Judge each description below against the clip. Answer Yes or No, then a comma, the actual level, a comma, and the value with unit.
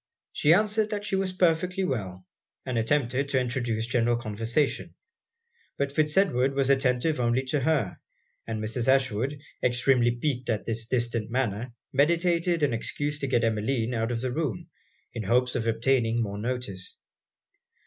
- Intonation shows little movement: No, average, 4.2 semitones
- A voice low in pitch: Yes, low, 125 Hz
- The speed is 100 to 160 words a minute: Yes, average, 155 wpm